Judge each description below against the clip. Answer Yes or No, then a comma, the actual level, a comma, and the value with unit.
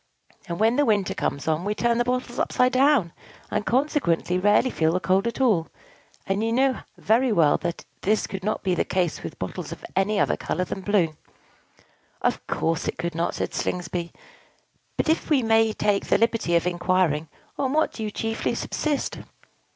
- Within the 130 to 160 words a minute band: No, average, 190 wpm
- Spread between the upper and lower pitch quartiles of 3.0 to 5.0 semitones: No, wide, 5.4 semitones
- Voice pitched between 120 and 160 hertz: No, high, 205 Hz